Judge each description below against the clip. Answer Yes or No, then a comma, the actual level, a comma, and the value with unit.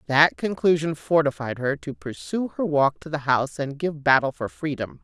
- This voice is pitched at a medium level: Yes, medium, 150 Hz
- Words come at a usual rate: Yes, average, 190 wpm